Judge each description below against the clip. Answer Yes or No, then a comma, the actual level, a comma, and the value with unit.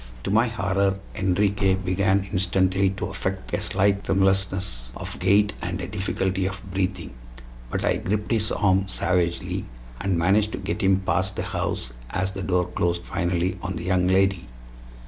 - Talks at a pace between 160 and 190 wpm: Yes, average, 165 wpm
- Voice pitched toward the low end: Yes, very low, 95 Hz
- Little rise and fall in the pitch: Yes, narrow, 1.4 semitones